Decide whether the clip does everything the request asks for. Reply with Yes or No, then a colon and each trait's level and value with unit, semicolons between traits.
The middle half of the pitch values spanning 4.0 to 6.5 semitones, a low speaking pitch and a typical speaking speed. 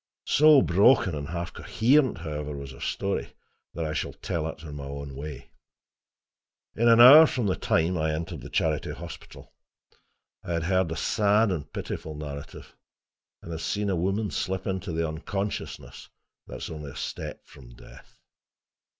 Yes: average, 4.8 semitones; very low, 85 Hz; average, 165 wpm